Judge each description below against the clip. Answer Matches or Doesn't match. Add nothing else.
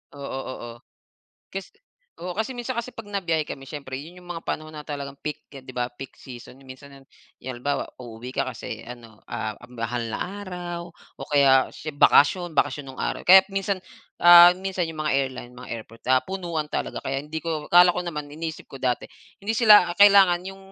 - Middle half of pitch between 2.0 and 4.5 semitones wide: Doesn't match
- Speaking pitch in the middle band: Matches